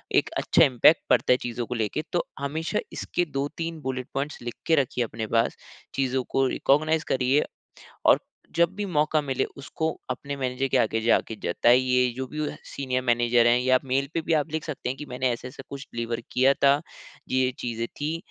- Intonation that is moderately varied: Yes, average, 3.2 semitones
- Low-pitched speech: Yes, low, 130 Hz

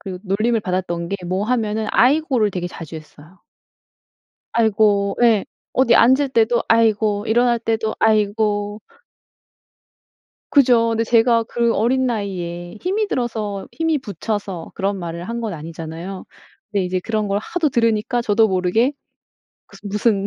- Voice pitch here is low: No, high, 215 Hz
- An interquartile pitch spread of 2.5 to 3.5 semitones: Yes, average, 3.2 semitones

